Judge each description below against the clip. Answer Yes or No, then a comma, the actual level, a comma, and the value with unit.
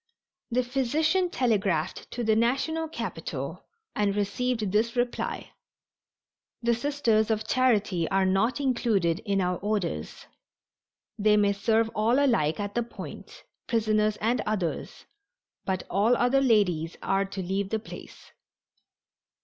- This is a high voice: Yes, high, 215 Hz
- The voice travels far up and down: No, average, 3.7 semitones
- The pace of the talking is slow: Yes, slow, 125 wpm